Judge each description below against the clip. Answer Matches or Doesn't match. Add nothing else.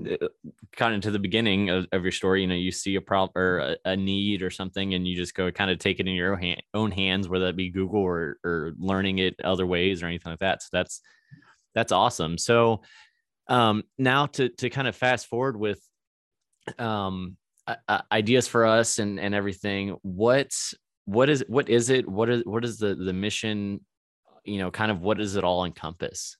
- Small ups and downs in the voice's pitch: Doesn't match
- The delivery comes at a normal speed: Doesn't match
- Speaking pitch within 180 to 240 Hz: Doesn't match